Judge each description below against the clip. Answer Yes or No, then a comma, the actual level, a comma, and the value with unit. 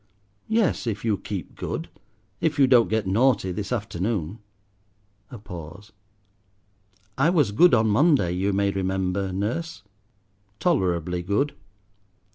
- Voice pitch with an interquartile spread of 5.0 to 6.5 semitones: Yes, wide, 5.4 semitones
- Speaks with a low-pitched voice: Yes, low, 105 Hz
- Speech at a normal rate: No, slow, 120 wpm